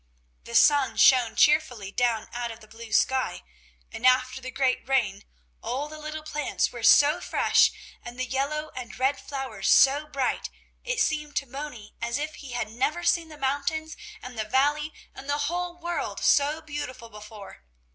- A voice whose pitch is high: Yes, very high, 270 Hz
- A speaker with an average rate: Yes, average, 175 wpm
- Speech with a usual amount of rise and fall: Yes, average, 3.9 semitones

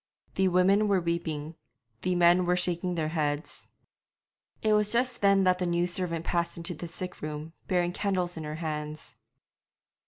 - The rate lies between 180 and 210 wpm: No, average, 165 wpm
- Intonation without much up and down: Yes, narrow, 2.1 semitones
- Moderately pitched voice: Yes, medium, 175 Hz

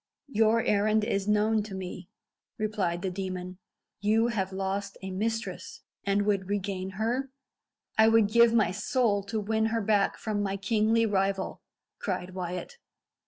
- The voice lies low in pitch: No, high, 205 Hz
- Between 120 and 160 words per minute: Yes, average, 150 wpm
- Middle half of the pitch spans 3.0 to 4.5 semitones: No, narrow, 2.4 semitones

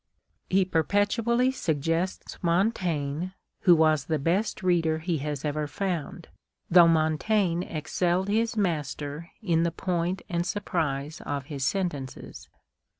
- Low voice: No, medium, 170 Hz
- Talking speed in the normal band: No, slow, 120 wpm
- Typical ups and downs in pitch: Yes, average, 3.5 semitones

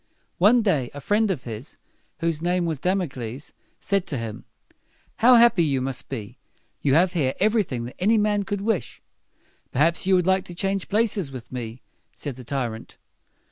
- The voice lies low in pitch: No, medium, 170 Hz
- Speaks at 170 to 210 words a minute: Yes, average, 180 wpm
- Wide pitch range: Yes, wide, 7.2 semitones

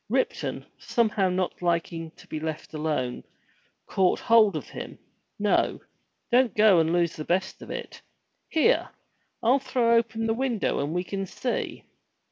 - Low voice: No, high, 190 Hz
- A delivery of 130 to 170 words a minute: Yes, average, 150 wpm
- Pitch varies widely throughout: Yes, wide, 5.7 semitones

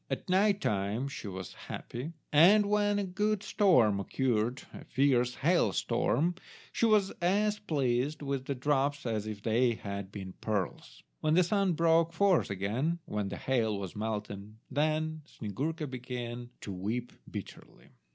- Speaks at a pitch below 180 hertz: Yes, low, 135 Hz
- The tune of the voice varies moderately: No, wide, 7.8 semitones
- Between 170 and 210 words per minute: No, average, 145 wpm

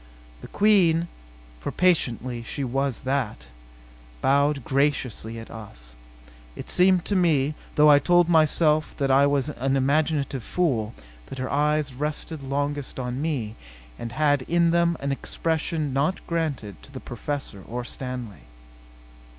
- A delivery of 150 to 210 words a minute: No, average, 140 wpm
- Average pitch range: Yes, average, 3.6 semitones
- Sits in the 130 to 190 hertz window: Yes, medium, 140 Hz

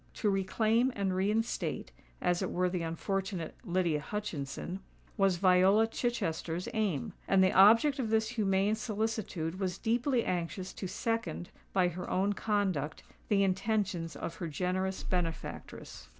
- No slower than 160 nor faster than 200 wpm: No, slow, 135 wpm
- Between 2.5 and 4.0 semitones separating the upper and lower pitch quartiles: Yes, average, 3.4 semitones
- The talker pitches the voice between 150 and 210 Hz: Yes, high, 190 Hz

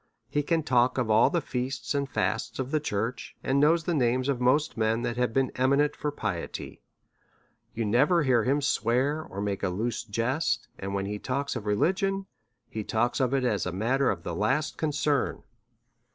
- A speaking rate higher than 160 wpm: Yes, average, 195 wpm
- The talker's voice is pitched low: Yes, low, 125 Hz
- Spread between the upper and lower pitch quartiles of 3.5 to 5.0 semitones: Yes, average, 4.6 semitones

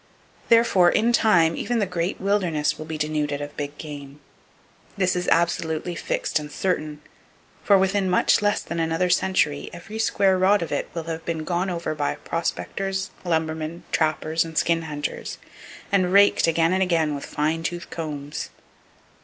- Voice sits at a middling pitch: Yes, medium, 170 Hz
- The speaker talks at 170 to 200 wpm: No, average, 160 wpm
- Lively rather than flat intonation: No, average, 3.3 semitones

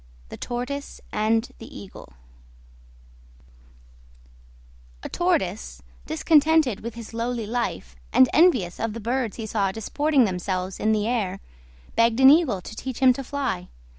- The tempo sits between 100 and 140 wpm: Yes, slow, 135 wpm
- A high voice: Yes, high, 230 Hz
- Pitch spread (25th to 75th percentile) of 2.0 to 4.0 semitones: No, average, 4.6 semitones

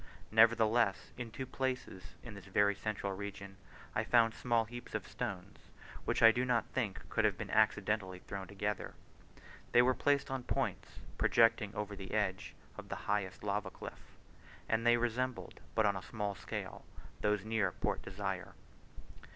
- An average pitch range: Yes, average, 3.0 semitones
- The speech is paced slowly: No, average, 160 wpm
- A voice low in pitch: Yes, low, 105 Hz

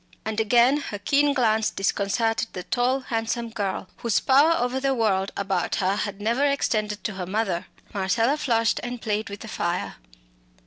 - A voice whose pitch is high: Yes, high, 225 Hz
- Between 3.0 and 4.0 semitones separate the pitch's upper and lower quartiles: Yes, average, 3.6 semitones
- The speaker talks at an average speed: Yes, average, 170 wpm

